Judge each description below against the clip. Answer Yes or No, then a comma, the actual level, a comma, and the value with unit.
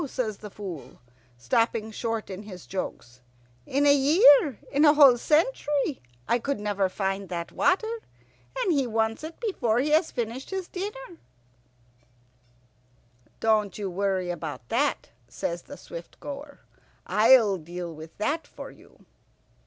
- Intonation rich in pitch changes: Yes, wide, 7.3 semitones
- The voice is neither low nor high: No, high, 225 Hz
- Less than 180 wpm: Yes, average, 140 wpm